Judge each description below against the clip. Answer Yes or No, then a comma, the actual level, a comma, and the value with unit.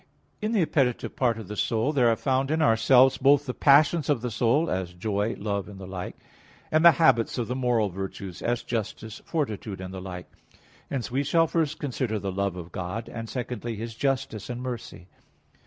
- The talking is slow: No, average, 200 wpm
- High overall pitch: No, low, 115 Hz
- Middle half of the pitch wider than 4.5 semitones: Yes, average, 4.9 semitones